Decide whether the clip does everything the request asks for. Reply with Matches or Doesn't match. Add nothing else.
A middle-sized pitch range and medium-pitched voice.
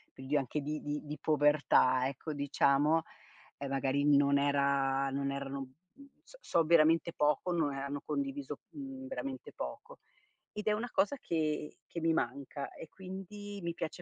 Matches